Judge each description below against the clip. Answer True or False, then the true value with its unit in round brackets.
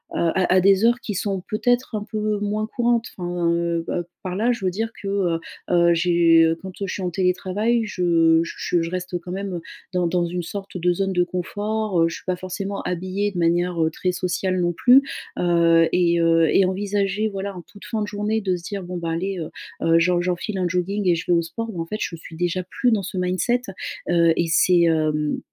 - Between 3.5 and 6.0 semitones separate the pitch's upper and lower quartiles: False (2.9 semitones)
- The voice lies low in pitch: False (180 Hz)